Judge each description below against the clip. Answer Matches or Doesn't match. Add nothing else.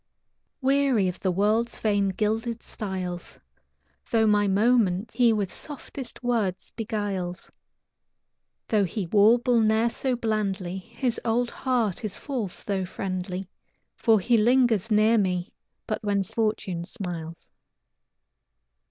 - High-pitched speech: Matches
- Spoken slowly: Matches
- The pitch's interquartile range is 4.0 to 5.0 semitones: Doesn't match